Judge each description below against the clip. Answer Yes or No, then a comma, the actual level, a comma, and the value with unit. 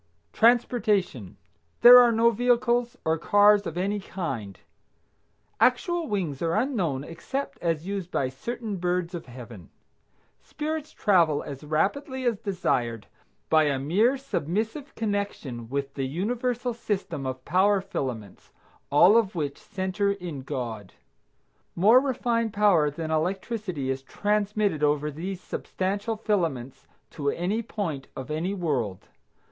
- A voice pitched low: No, medium, 185 Hz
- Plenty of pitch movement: Yes, wide, 7.1 semitones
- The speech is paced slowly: Yes, slow, 130 wpm